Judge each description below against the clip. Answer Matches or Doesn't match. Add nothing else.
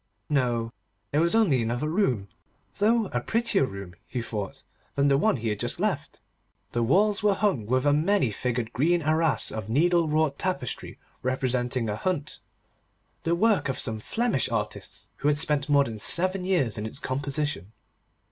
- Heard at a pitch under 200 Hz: Matches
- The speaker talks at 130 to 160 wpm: Doesn't match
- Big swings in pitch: Matches